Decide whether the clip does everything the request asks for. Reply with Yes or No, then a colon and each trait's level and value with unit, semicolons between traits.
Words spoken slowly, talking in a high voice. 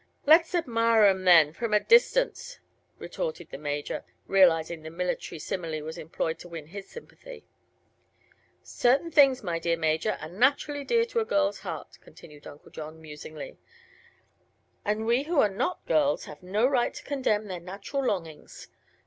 No: average, 155 wpm; high, 200 Hz